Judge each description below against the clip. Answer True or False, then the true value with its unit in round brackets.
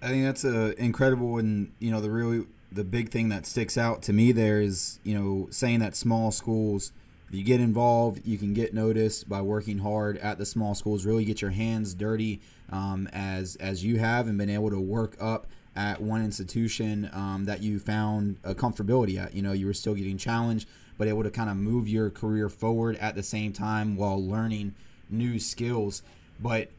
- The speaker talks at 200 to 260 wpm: True (205 wpm)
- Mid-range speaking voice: False (105 Hz)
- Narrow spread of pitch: True (2.1 semitones)